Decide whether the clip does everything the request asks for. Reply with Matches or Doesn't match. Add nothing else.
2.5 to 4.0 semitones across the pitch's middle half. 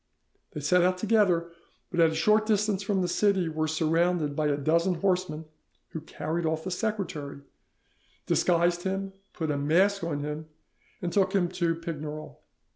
Matches